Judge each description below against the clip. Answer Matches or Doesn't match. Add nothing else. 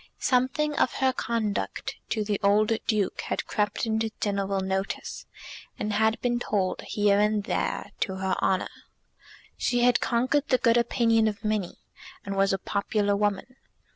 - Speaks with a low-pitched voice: Doesn't match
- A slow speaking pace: Doesn't match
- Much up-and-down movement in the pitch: Doesn't match